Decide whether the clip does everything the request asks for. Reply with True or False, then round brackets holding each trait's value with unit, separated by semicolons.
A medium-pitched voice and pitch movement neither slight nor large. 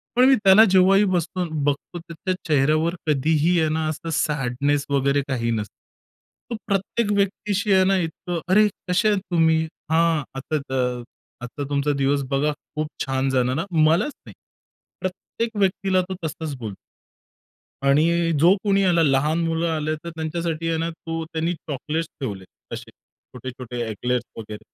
True (160 Hz; 4.5 semitones)